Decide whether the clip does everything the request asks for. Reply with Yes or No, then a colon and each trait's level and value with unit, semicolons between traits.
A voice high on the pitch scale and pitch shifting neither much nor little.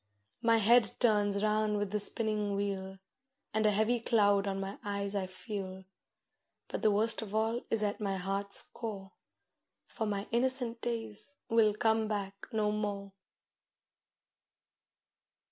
No: high, 210 Hz; narrow, 1.9 semitones